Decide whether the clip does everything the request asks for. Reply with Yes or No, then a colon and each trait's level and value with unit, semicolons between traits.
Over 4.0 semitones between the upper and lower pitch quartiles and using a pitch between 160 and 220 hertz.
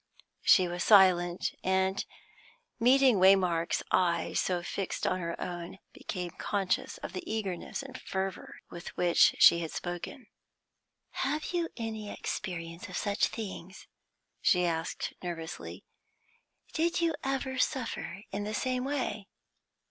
Yes: average, 4.7 semitones; high, 190 Hz